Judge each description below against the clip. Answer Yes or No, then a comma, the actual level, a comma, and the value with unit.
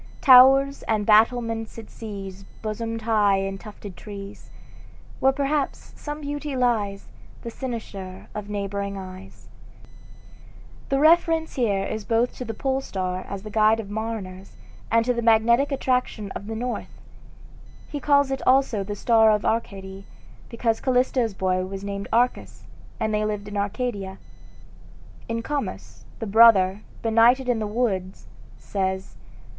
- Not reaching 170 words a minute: Yes, average, 140 wpm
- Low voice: No, high, 220 Hz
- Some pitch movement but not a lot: Yes, average, 3.8 semitones